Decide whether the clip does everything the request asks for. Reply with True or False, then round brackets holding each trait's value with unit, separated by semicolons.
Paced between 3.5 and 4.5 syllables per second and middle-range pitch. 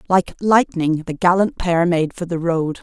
True (4.3 syllables/s; 175 Hz)